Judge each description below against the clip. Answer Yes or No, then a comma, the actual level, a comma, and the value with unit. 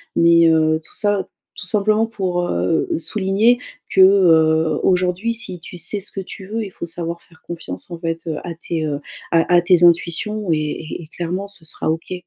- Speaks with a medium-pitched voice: Yes, medium, 175 Hz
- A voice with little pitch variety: No, average, 3.1 semitones